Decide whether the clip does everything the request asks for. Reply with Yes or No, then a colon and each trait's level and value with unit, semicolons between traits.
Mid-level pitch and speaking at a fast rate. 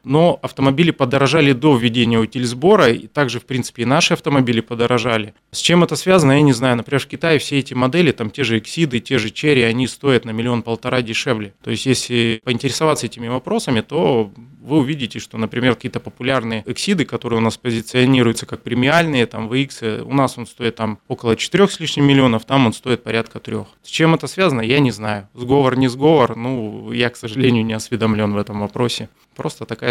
No: low, 125 Hz; fast, 195 wpm